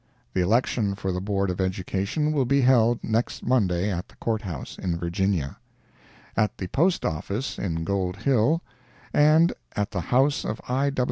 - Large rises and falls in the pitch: Yes, wide, 5.8 semitones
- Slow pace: No, average, 160 wpm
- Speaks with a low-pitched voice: Yes, low, 105 Hz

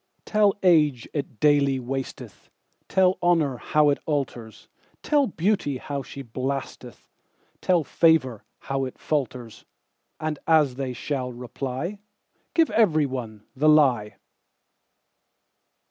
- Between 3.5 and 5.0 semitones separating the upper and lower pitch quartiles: Yes, average, 4.2 semitones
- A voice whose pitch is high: No, medium, 140 Hz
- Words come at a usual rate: No, slow, 95 wpm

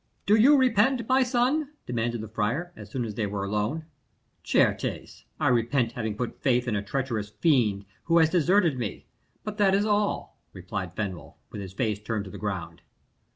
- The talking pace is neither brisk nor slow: Yes, average, 185 wpm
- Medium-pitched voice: No, low, 120 Hz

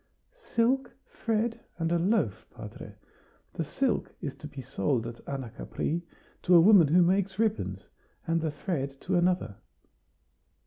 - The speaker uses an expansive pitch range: Yes, wide, 6.4 semitones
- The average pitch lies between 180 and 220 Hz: No, medium, 170 Hz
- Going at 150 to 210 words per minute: No, average, 140 wpm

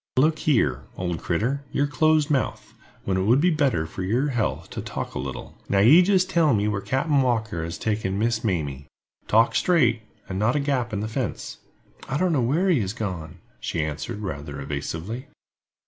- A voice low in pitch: Yes, low, 110 Hz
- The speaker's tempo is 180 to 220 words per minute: Yes, average, 195 wpm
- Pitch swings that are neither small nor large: No, wide, 7.4 semitones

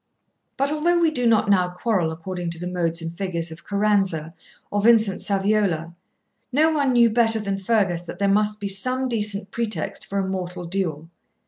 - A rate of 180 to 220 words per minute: Yes, average, 185 wpm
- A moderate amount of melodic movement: Yes, average, 4.1 semitones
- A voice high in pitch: Yes, high, 200 Hz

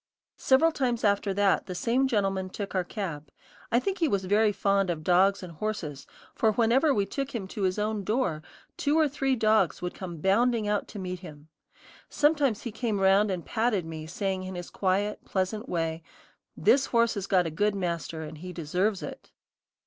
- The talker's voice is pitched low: No, high, 200 Hz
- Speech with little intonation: No, average, 3.8 semitones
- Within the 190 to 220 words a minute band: Yes, average, 195 wpm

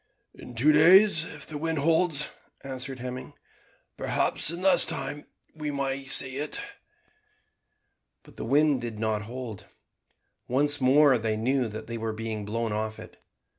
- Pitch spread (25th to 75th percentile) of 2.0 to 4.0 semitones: No, average, 4.7 semitones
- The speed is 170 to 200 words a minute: No, average, 150 wpm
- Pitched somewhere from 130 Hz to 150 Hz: Yes, low, 135 Hz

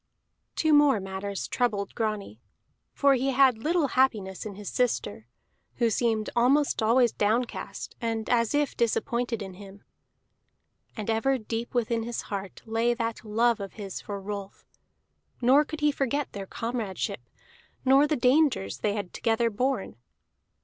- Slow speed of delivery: No, average, 145 wpm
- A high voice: Yes, high, 230 Hz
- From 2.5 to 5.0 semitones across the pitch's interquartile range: Yes, average, 3.9 semitones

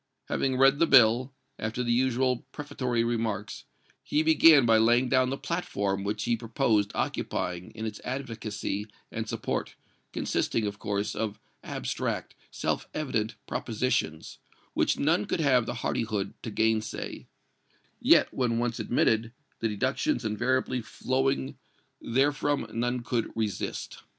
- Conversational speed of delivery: No, slow, 130 wpm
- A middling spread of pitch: Yes, average, 3.1 semitones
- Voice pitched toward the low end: Yes, low, 120 Hz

